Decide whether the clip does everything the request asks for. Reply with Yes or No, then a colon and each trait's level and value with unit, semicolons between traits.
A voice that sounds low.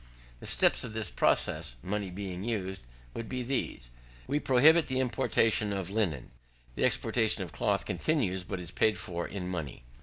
Yes: low, 100 Hz